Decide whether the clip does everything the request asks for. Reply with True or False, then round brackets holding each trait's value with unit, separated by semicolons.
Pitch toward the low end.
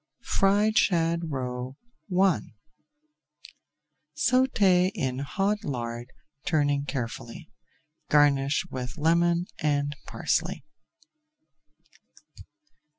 False (150 Hz)